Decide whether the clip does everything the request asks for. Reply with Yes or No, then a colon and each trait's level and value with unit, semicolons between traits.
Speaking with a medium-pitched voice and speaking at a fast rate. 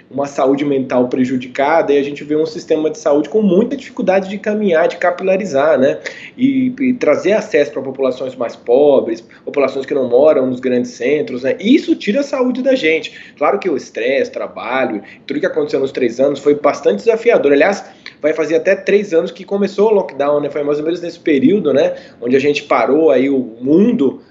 Yes: medium, 180 Hz; fast, 200 wpm